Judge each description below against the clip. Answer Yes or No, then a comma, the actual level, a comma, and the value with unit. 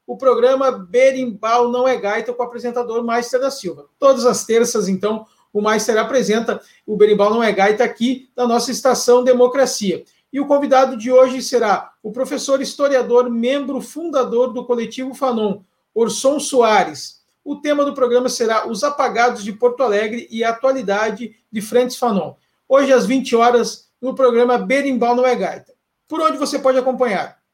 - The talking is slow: No, average, 165 wpm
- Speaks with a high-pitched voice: Yes, high, 245 Hz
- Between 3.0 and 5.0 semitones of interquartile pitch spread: No, narrow, 2.4 semitones